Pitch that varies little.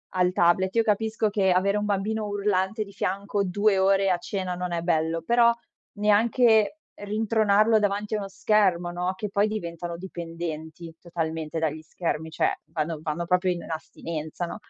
No: average, 3.5 semitones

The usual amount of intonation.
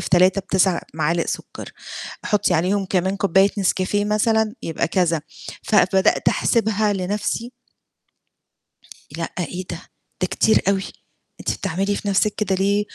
No: narrow, 2.3 semitones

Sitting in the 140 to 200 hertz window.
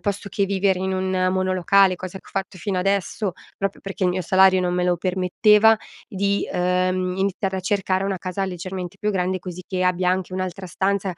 Yes: medium, 185 Hz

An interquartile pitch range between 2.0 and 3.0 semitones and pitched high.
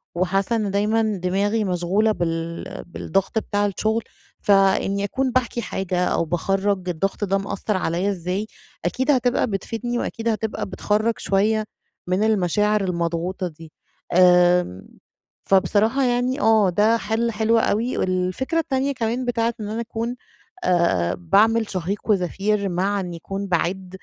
No: average, 3.5 semitones; high, 200 Hz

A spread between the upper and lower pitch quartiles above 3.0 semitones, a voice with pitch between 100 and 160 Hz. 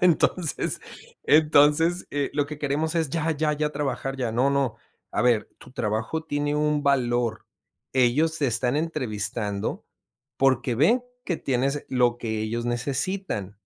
Yes: average, 4.0 semitones; medium, 140 Hz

